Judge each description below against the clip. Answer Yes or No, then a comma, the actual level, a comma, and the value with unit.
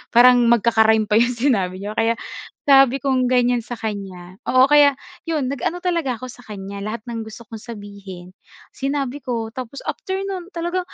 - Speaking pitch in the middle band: No, high, 240 Hz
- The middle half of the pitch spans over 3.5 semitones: Yes, average, 4.2 semitones